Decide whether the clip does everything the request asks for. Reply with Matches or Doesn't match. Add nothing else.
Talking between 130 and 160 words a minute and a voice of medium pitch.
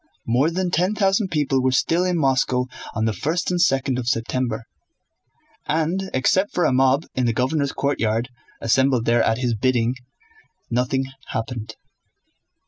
Doesn't match